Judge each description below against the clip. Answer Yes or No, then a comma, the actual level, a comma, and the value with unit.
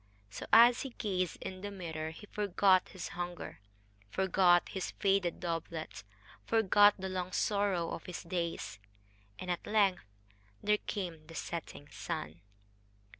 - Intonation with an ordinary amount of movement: Yes, average, 3.1 semitones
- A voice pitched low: No, medium, 185 Hz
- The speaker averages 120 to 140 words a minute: Yes, slow, 135 wpm